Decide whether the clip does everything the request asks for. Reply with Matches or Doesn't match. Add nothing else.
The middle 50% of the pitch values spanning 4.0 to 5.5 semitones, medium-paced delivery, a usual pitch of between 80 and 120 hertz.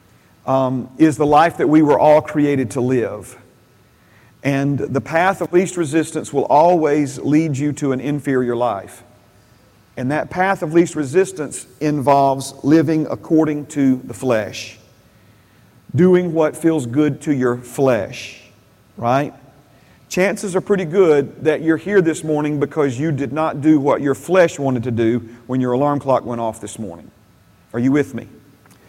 Doesn't match